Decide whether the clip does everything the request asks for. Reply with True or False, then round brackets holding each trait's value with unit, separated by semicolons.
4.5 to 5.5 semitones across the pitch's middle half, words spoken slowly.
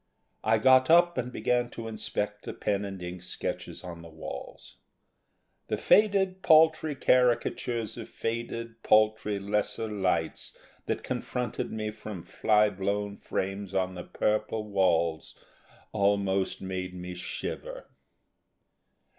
False (3.8 semitones; 120 wpm)